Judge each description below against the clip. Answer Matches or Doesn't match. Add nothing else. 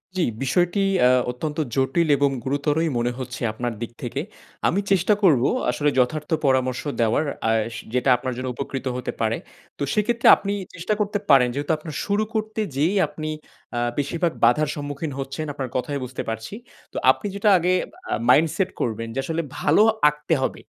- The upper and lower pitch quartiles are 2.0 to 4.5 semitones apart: Doesn't match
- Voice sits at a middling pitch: Matches